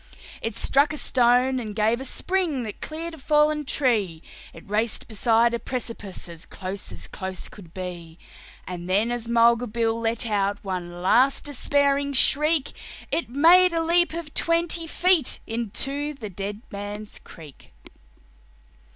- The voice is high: Yes, high, 235 Hz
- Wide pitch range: Yes, wide, 6.3 semitones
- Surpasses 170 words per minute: No, average, 150 wpm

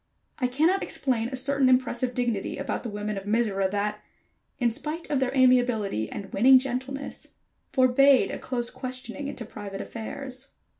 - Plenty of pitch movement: No, average, 3.5 semitones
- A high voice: Yes, very high, 250 Hz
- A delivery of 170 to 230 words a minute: No, average, 155 wpm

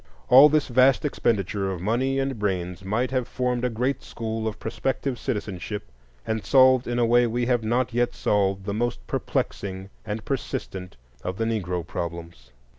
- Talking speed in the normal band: Yes, average, 170 wpm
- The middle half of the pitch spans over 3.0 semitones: Yes, average, 4.5 semitones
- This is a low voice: Yes, low, 115 Hz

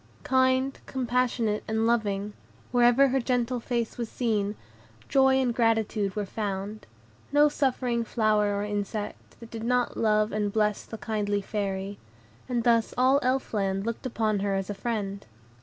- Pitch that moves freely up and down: No, average, 3.1 semitones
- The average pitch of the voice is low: No, high, 225 Hz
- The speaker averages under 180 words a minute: Yes, average, 155 wpm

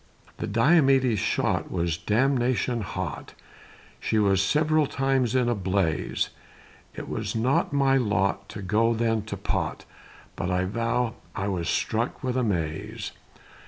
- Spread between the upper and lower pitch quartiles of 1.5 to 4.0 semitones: No, average, 4.7 semitones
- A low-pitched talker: Yes, low, 115 Hz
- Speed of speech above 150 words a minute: No, slow, 135 wpm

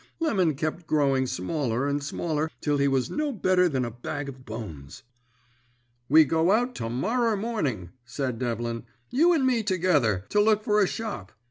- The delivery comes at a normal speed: Yes, average, 170 wpm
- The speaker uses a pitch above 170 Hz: No, medium, 150 Hz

